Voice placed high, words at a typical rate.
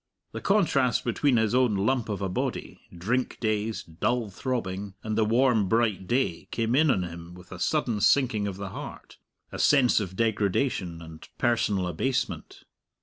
No: low, 110 Hz; average, 165 wpm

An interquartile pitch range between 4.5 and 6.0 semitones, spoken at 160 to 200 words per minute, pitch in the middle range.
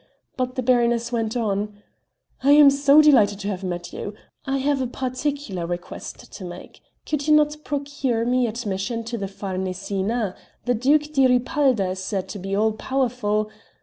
No: average, 5.3 semitones; average, 170 wpm; high, 235 Hz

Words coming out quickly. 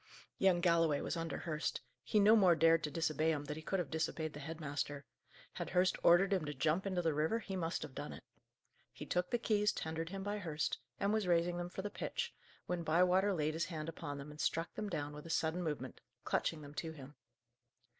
Yes: fast, 225 wpm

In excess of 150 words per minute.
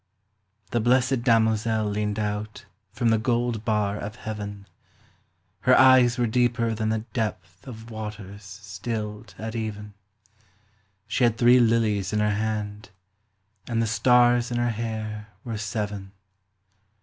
No: slow, 135 wpm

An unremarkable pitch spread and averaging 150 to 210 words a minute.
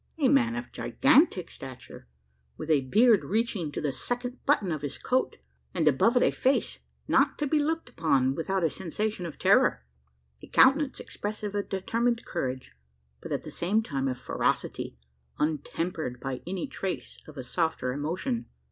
No: wide, 8.5 semitones; average, 165 wpm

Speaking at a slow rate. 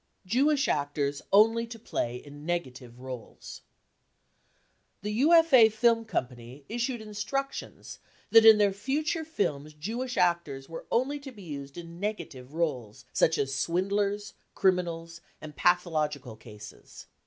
Yes: slow, 125 wpm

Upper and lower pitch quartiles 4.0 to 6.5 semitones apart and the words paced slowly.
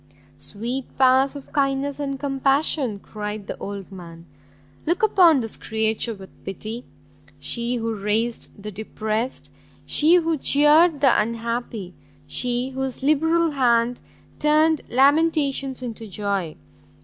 Yes: average, 4.7 semitones; slow, 120 wpm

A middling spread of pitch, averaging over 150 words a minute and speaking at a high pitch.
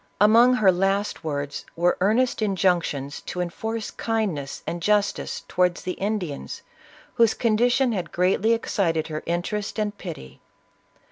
No: average, 4.2 semitones; slow, 135 wpm; high, 195 Hz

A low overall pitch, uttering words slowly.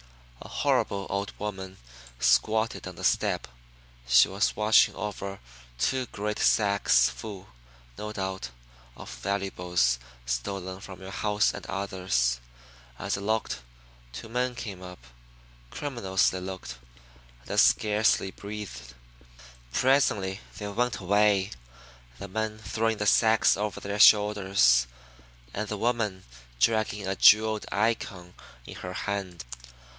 Yes: low, 100 Hz; slow, 125 wpm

